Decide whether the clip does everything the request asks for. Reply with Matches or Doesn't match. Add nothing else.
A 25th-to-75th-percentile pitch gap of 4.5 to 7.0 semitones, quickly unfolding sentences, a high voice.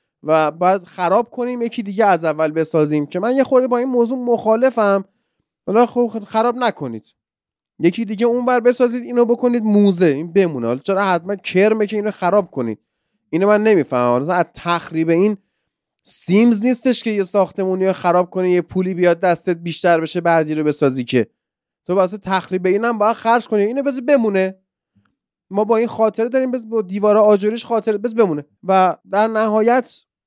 Matches